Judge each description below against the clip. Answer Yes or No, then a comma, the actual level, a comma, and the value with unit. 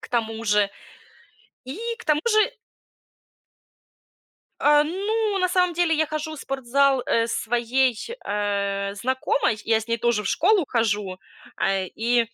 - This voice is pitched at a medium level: No, high, 245 Hz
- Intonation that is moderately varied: No, wide, 6.2 semitones